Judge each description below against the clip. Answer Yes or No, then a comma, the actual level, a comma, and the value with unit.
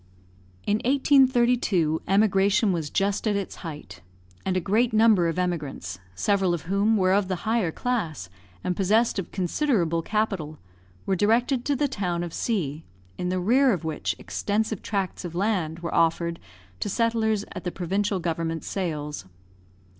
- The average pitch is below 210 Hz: Yes, high, 190 Hz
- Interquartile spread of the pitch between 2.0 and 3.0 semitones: No, average, 4.5 semitones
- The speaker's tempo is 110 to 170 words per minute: Yes, average, 155 wpm